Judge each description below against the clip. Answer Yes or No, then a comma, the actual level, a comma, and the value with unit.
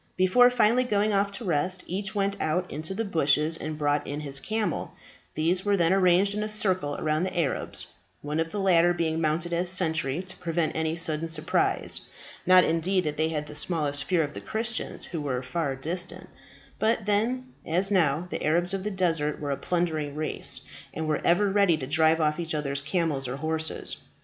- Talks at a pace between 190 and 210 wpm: Yes, average, 200 wpm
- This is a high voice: No, medium, 165 Hz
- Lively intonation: No, average, 3.8 semitones